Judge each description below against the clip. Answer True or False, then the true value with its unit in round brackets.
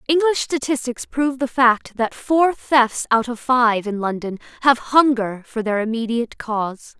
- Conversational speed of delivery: True (165 wpm)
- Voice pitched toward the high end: True (245 Hz)